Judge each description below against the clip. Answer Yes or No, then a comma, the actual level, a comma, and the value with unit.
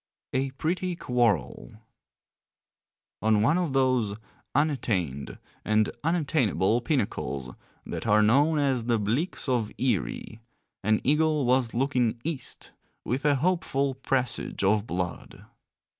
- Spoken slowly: Yes, slow, 115 wpm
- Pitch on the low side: Yes, low, 125 Hz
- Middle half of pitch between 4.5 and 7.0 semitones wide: Yes, average, 5.1 semitones